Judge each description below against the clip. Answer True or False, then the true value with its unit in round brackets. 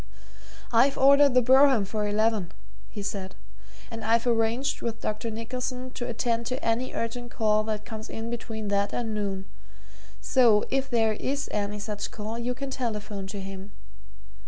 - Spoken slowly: False (160 wpm)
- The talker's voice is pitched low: False (225 Hz)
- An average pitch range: True (3.0 semitones)